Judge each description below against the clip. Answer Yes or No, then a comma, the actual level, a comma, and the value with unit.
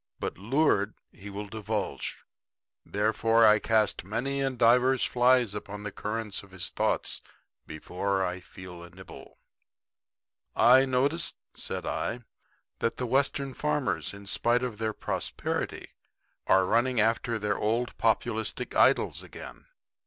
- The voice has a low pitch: Yes, low, 110 Hz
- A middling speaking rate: No, slow, 130 wpm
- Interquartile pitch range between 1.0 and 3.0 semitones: No, average, 3.7 semitones